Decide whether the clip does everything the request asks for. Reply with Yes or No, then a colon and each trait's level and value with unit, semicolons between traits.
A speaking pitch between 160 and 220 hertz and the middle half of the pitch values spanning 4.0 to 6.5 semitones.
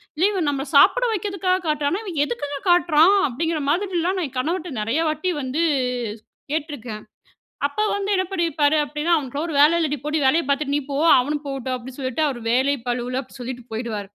No: very high, 295 Hz; average, 4.4 semitones